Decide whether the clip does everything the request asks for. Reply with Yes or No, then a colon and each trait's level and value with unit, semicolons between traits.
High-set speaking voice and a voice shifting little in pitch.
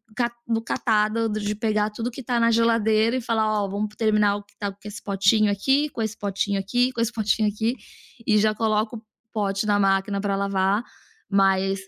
Yes: high, 215 Hz; narrow, 2.1 semitones